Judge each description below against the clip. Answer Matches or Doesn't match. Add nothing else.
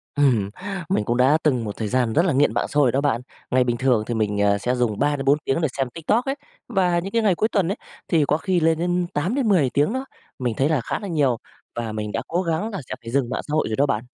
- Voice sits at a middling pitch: Matches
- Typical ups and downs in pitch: Doesn't match